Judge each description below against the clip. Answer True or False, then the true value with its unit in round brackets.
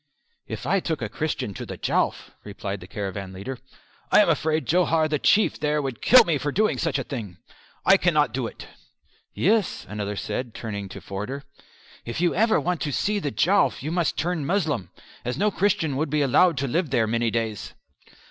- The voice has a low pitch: False (150 Hz)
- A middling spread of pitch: False (7.0 semitones)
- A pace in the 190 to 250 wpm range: True (195 wpm)